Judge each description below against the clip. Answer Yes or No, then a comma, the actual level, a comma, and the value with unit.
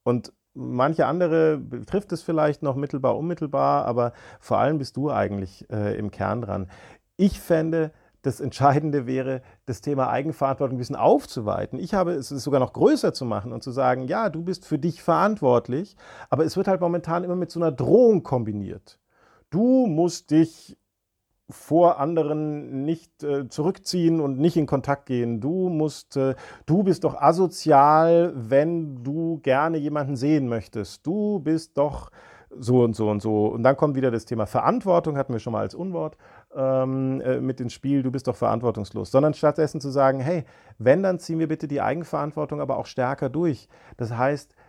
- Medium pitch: Yes, medium, 145 Hz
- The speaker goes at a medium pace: Yes, average, 180 wpm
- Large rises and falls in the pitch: No, average, 4.5 semitones